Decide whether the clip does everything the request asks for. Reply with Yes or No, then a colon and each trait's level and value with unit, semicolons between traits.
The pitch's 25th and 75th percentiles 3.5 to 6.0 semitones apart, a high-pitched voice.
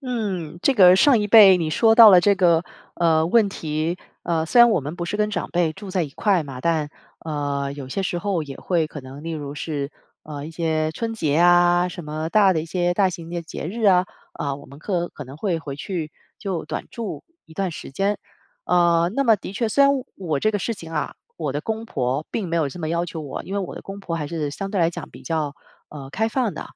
No: average, 4.1 semitones; medium, 170 Hz